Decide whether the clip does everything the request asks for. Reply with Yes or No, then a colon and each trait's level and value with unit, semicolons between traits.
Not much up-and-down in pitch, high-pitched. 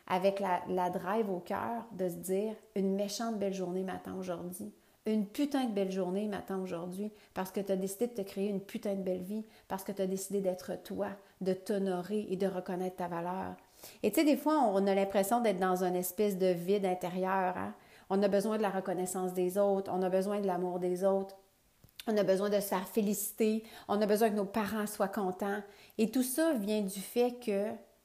Yes: narrow, 2.1 semitones; high, 195 Hz